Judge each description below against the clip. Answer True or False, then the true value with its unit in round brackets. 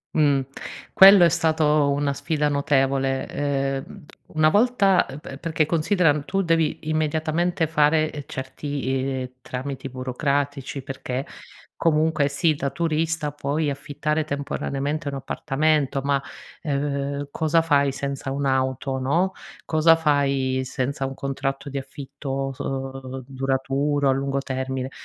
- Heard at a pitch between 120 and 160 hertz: True (140 Hz)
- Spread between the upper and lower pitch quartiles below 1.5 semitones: False (2.4 semitones)